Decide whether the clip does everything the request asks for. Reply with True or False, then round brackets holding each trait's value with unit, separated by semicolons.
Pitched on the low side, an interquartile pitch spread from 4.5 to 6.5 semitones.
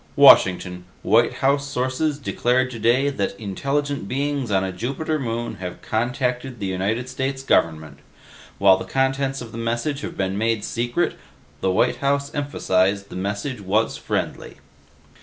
True (120 Hz; 5.6 semitones)